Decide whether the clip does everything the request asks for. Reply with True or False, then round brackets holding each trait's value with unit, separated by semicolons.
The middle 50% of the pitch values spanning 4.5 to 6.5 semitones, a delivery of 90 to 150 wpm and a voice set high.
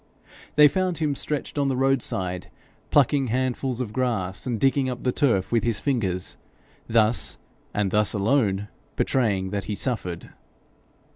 False (4.9 semitones; 145 wpm; 120 Hz)